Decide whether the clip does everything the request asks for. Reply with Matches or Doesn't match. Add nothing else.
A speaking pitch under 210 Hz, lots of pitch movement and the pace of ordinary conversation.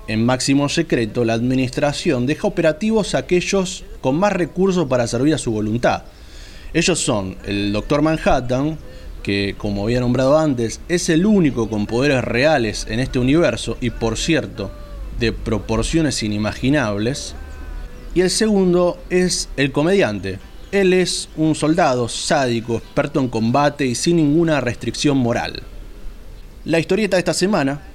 Matches